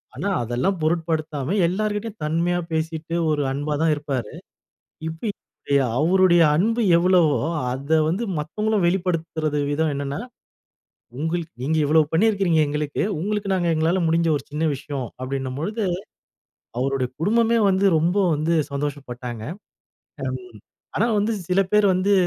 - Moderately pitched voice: Yes, medium, 160 Hz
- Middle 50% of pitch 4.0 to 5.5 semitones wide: Yes, average, 4.4 semitones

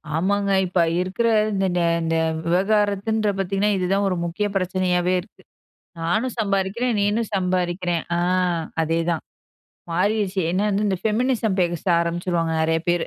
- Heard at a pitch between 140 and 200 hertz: Yes, high, 190 Hz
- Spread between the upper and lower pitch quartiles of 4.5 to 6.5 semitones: No, average, 2.9 semitones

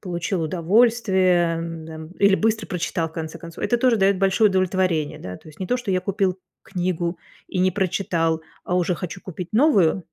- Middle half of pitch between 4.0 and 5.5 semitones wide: No, average, 2.9 semitones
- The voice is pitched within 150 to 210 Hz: Yes, medium, 185 Hz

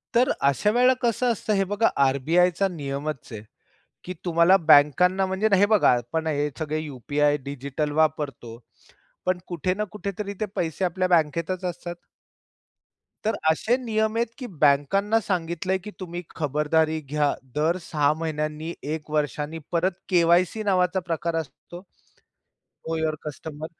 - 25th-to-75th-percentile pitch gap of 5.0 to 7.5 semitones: No, average, 4.1 semitones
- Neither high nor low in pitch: Yes, medium, 165 Hz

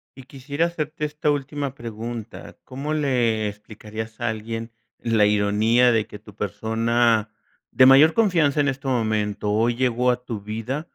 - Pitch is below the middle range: Yes, low, 120 Hz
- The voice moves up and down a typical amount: Yes, average, 3.8 semitones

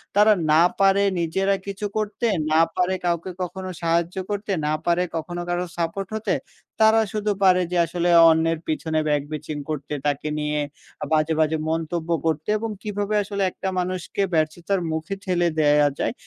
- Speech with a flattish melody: No, average, 3.6 semitones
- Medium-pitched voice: Yes, medium, 175 Hz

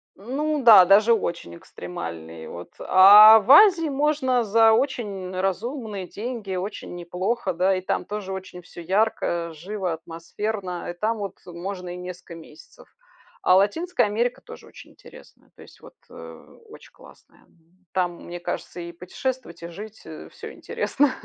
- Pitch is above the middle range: Yes, high, 195 Hz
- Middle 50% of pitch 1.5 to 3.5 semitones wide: No, average, 4.8 semitones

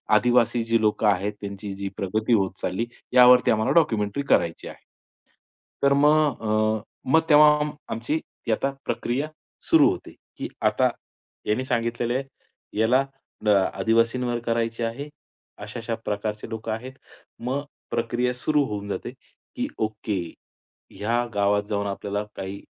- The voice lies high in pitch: No, low, 115 Hz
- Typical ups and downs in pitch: Yes, average, 3.1 semitones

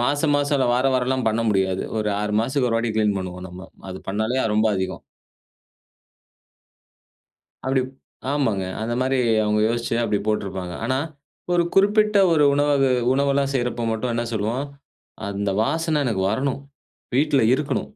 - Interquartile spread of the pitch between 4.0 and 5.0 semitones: Yes, average, 4.7 semitones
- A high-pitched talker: No, low, 120 Hz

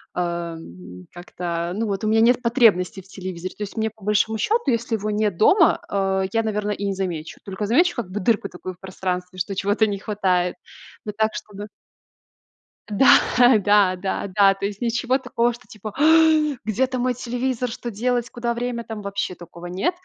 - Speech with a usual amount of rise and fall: Yes, average, 4.0 semitones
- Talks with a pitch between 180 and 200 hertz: No, high, 210 Hz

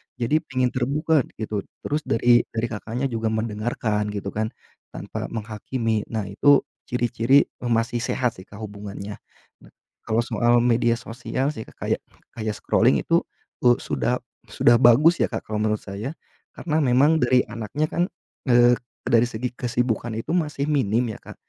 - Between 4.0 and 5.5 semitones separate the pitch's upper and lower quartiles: No, average, 2.7 semitones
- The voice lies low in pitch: Yes, low, 120 Hz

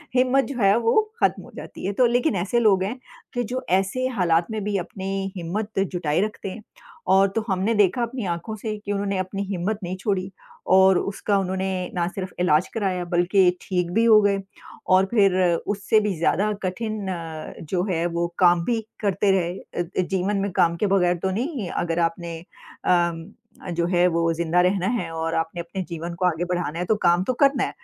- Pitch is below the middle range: No, high, 190 Hz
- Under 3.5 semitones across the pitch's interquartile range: Yes, average, 2.9 semitones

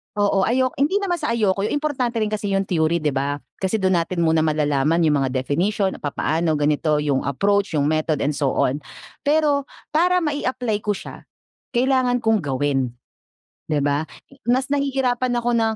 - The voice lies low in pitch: No, high, 195 Hz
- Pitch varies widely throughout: Yes, wide, 8.8 semitones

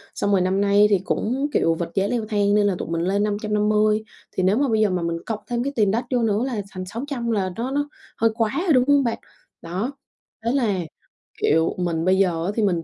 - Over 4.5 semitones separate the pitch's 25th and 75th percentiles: No, average, 3.8 semitones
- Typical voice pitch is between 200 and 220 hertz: Yes, high, 210 Hz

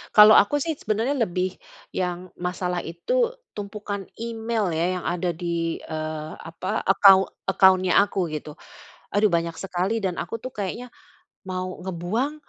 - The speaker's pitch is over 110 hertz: Yes, high, 190 Hz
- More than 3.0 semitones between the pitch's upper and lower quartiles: Yes, average, 3.5 semitones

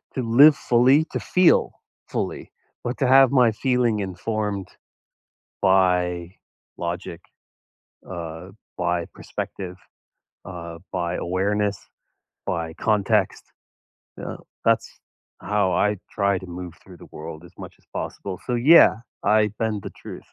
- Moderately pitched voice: No, low, 100 Hz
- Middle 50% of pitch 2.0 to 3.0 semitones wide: No, average, 4.4 semitones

